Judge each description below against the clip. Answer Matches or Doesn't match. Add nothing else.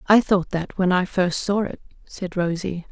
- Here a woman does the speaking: Matches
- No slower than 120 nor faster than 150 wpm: Doesn't match